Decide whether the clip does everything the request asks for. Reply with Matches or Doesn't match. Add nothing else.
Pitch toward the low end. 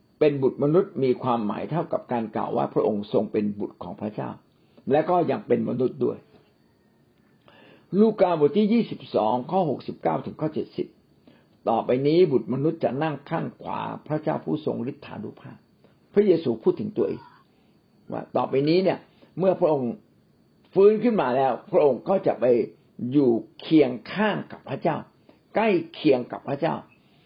Doesn't match